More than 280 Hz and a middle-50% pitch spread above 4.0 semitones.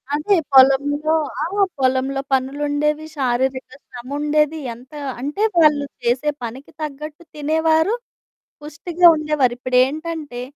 No: very high, 290 Hz; average, 2.7 semitones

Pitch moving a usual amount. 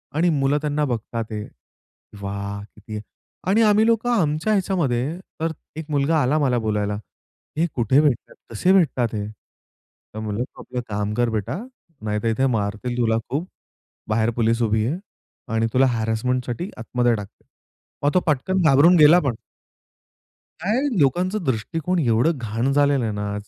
No: wide, 5.9 semitones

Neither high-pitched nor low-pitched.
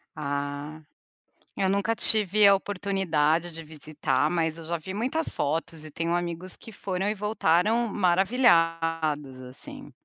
Yes: medium, 170 Hz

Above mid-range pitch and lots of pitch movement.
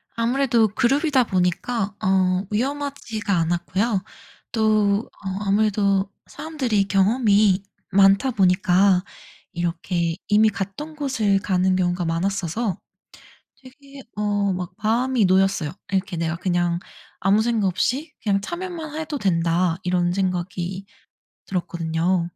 No: high, 195 Hz; average, 4.1 semitones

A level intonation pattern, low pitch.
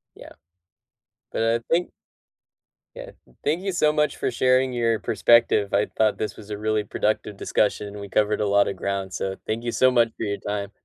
No: average, 3.0 semitones; low, 110 Hz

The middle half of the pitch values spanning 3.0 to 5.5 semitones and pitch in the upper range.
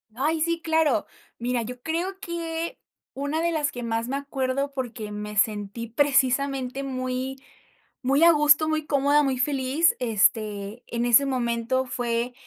Yes: average, 3.9 semitones; very high, 265 Hz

